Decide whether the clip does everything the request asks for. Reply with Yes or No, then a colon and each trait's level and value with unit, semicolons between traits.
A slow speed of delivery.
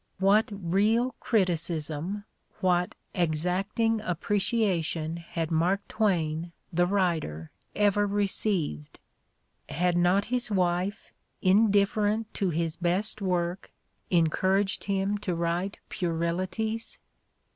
Yes: slow, 90 wpm